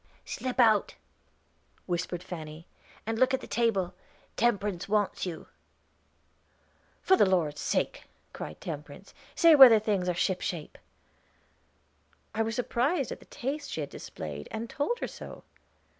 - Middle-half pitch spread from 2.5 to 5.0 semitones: No, wide, 5.6 semitones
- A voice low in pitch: No, high, 210 Hz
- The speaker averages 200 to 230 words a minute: No, average, 140 wpm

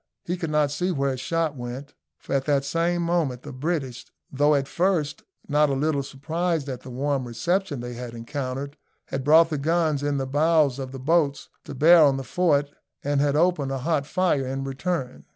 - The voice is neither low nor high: Yes, medium, 145 Hz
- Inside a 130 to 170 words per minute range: No, fast, 205 wpm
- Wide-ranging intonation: No, average, 3.4 semitones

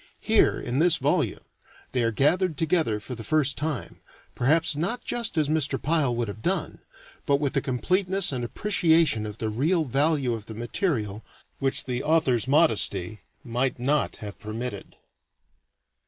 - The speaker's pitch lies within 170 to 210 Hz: No, low, 135 Hz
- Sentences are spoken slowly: No, average, 155 wpm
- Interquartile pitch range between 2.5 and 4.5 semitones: No, wide, 5.4 semitones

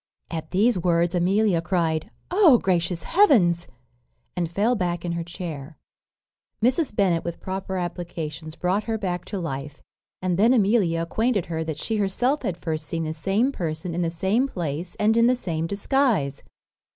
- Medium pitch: Yes, medium, 180 Hz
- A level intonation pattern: No, average, 4.2 semitones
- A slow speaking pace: No, average, 165 wpm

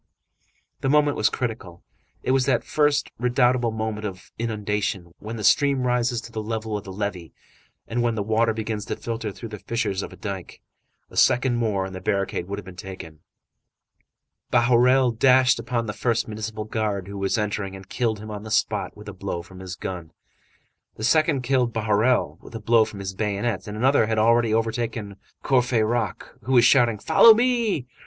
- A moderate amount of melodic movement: Yes, average, 3.2 semitones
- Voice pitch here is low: Yes, low, 110 Hz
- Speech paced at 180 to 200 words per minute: Yes, average, 185 wpm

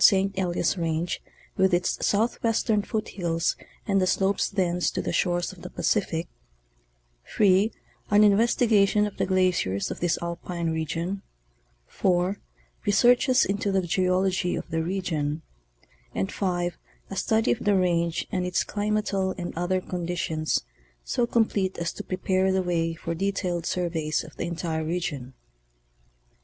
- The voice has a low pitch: No, medium, 180 Hz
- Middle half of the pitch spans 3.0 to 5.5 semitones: No, narrow, 2.6 semitones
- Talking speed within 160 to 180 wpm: No, average, 145 wpm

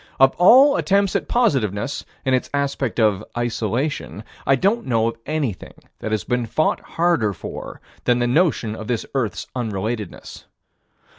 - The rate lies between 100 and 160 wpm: Yes, average, 150 wpm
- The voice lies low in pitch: Yes, low, 125 Hz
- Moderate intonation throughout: No, wide, 5.8 semitones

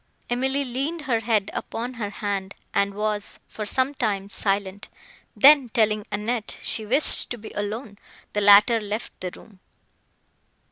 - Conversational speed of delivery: Yes, average, 145 wpm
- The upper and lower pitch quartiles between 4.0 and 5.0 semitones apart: No, average, 3.1 semitones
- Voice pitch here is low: No, high, 215 Hz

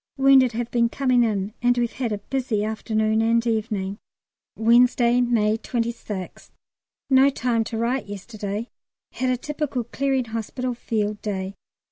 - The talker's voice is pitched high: Yes, high, 235 Hz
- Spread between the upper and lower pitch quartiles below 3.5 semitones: Yes, narrow, 2.5 semitones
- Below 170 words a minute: Yes, average, 140 wpm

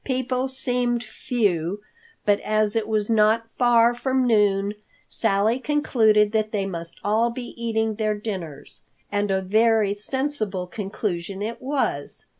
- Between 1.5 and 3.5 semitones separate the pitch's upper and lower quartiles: Yes, average, 2.8 semitones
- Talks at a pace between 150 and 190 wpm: No, slow, 135 wpm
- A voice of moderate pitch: No, high, 215 Hz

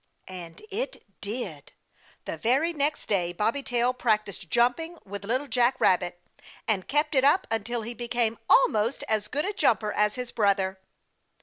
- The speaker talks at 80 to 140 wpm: No, average, 160 wpm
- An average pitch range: Yes, average, 4.5 semitones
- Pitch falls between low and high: No, high, 235 Hz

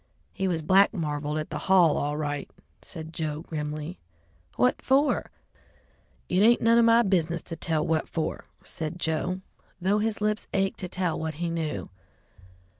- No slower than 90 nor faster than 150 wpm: No, average, 165 wpm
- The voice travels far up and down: No, average, 3.8 semitones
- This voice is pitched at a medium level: Yes, medium, 170 Hz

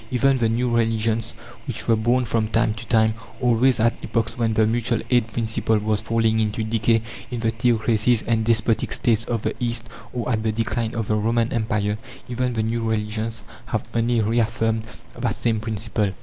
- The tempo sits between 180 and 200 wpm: Yes, average, 185 wpm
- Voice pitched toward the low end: Yes, low, 115 Hz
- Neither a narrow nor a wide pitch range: No, narrow, 1.2 semitones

